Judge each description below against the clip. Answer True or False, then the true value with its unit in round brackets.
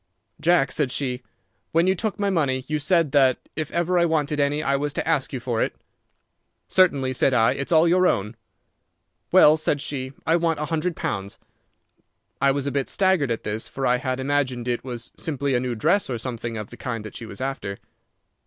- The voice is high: False (140 Hz)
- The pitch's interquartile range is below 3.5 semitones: False (4.2 semitones)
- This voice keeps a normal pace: False (210 wpm)